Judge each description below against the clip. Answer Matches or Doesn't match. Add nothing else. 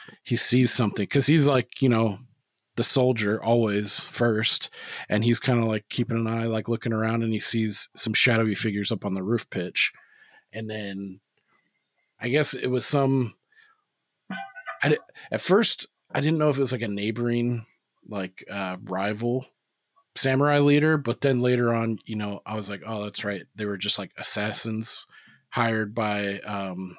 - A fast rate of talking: Doesn't match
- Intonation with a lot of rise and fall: Doesn't match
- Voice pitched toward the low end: Matches